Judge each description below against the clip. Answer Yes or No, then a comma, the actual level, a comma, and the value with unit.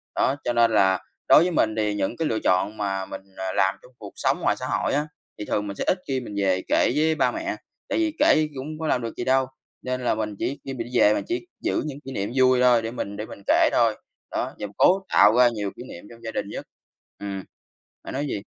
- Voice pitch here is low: Yes, low, 120 Hz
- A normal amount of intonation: Yes, average, 4.9 semitones